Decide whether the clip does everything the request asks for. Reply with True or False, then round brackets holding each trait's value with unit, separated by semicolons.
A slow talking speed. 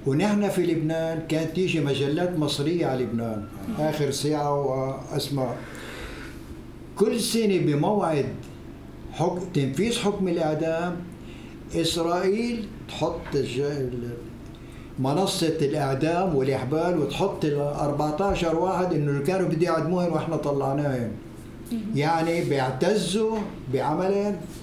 True (95 wpm)